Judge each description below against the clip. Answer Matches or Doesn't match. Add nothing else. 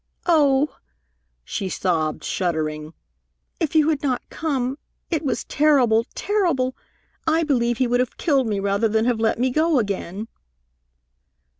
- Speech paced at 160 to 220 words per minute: Doesn't match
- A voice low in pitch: Doesn't match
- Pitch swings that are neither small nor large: Doesn't match